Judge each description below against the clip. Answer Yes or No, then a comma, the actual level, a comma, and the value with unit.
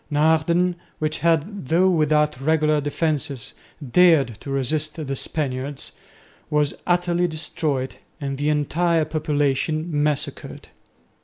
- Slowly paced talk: Yes, slow, 105 wpm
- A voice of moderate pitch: Yes, medium, 155 Hz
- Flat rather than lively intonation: Yes, narrow, 2.3 semitones